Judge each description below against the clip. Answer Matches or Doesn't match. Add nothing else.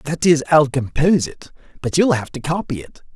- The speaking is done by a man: Matches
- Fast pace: Matches